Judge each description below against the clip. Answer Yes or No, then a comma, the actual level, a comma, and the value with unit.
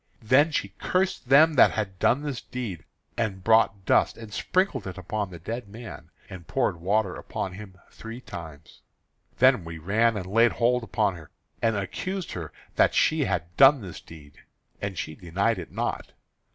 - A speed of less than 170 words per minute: No, average, 175 wpm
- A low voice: Yes, low, 105 Hz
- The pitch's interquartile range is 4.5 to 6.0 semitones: Yes, average, 4.8 semitones